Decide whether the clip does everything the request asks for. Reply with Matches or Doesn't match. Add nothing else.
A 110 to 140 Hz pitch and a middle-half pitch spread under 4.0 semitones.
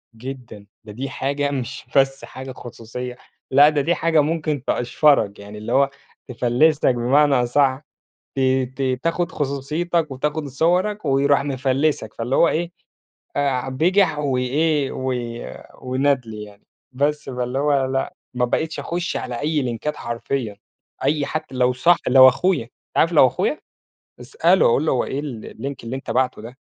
Matches